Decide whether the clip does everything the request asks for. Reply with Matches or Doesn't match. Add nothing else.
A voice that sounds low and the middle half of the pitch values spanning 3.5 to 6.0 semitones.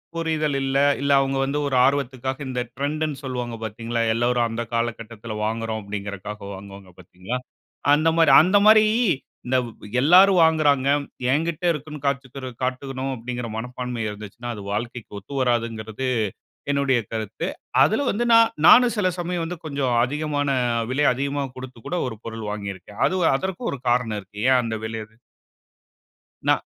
Matches